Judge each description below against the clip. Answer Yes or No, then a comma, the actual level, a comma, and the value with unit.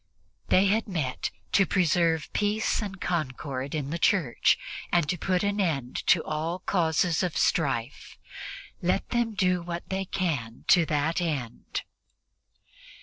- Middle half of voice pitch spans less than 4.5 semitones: Yes, average, 4.1 semitones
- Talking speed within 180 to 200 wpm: No, average, 140 wpm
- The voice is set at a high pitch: No, medium, 170 Hz